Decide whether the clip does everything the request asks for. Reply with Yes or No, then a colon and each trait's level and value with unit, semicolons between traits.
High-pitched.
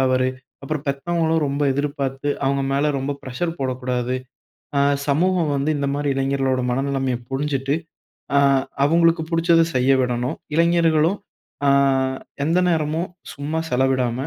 No: medium, 140 Hz